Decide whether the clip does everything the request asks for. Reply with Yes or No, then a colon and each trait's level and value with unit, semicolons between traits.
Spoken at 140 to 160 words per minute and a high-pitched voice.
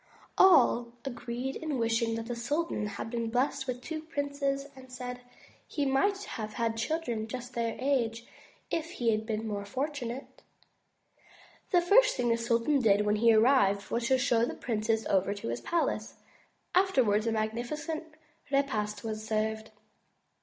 Yes: average, 155 wpm; high, 240 Hz